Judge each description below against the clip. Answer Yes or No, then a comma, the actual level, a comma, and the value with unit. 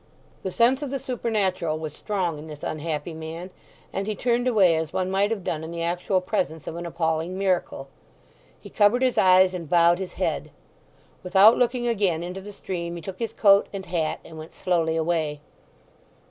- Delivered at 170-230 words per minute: Yes, average, 190 wpm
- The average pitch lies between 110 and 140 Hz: No, medium, 180 Hz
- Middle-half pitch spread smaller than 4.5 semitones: Yes, average, 3.7 semitones